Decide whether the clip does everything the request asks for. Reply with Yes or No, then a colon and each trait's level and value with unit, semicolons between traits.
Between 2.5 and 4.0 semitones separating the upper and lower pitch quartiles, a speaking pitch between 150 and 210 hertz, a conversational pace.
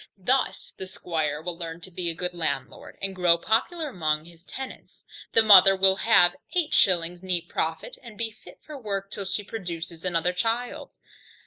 No: average, 4.4 semitones; medium, 185 Hz; average, 180 wpm